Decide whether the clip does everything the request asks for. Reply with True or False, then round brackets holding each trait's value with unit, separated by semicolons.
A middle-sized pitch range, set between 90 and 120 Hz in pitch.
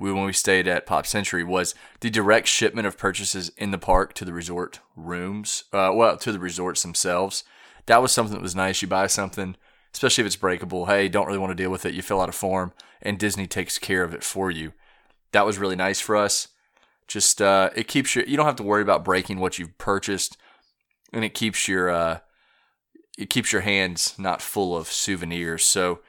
False (2.0 semitones; 95 Hz)